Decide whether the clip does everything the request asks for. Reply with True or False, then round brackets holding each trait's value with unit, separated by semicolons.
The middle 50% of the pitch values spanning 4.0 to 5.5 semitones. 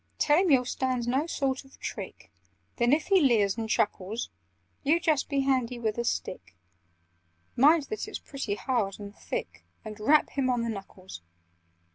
True (4.4 semitones)